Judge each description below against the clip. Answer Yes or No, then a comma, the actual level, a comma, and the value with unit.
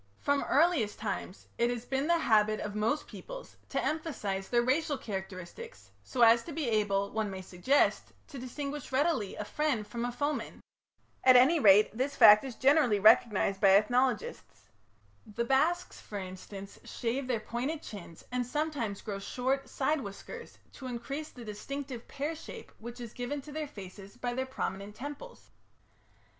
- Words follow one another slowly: No, average, 165 wpm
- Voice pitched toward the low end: No, high, 245 Hz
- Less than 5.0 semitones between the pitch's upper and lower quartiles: No, wide, 5.4 semitones